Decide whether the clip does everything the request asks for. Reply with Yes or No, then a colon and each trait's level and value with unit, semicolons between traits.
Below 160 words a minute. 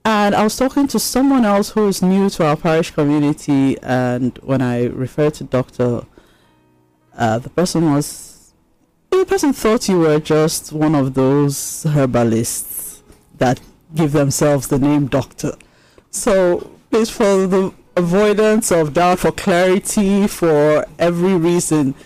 Yes: average, 140 wpm